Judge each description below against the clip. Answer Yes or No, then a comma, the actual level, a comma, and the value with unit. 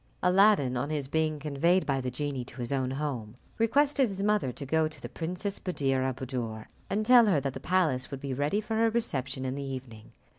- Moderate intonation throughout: No, wide, 6.3 semitones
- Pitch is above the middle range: No, medium, 145 Hz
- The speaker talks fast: Yes, fast, 220 wpm